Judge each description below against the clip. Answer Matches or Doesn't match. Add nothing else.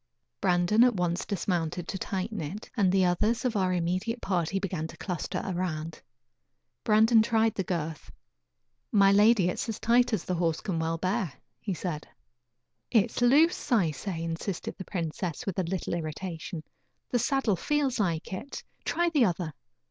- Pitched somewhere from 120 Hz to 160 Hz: Doesn't match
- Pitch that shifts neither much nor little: Matches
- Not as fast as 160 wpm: Doesn't match